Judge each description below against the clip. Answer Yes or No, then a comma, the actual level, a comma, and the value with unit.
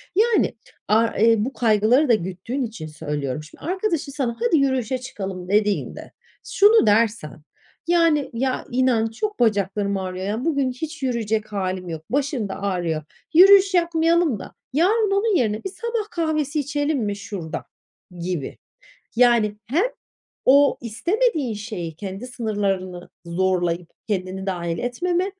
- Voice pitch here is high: Yes, high, 230 Hz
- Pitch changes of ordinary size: No, wide, 7.8 semitones